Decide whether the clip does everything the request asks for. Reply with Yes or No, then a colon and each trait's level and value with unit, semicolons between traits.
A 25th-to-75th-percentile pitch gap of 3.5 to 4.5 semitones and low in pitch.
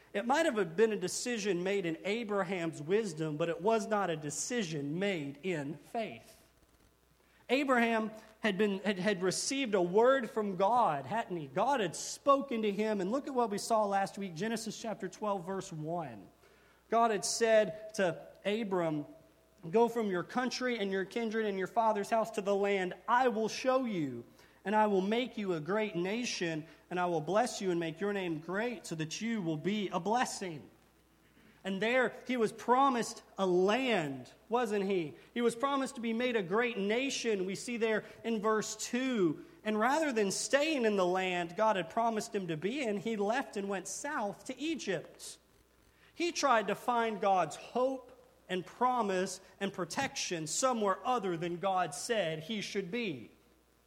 No: average, 3.9 semitones; high, 210 Hz